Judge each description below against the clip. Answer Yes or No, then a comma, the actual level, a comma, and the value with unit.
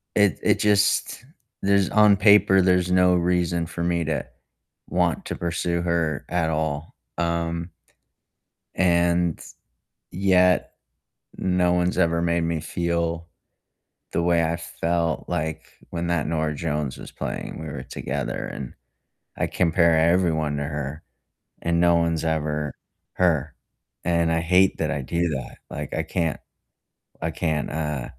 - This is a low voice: Yes, very low, 85 Hz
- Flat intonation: Yes, narrow, 1.9 semitones